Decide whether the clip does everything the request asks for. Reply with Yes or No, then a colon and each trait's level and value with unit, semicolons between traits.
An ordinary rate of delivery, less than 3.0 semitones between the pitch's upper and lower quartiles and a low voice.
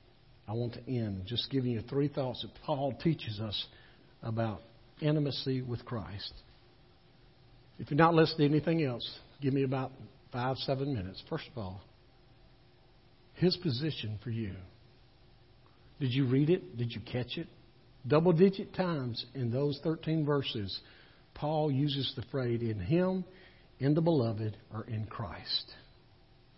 No: average, 145 wpm; average, 4.0 semitones; low, 125 Hz